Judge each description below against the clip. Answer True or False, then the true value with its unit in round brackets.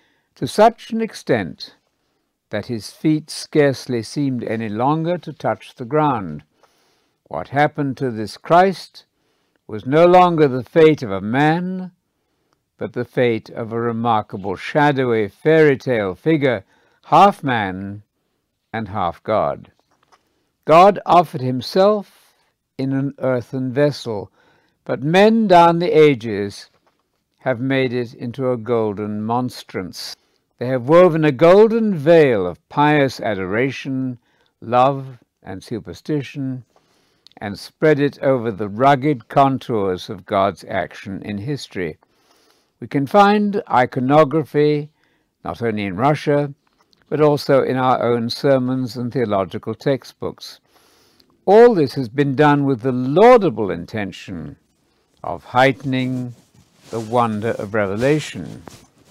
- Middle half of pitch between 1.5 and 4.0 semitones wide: False (4.4 semitones)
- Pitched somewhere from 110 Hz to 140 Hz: True (135 Hz)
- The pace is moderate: False (120 wpm)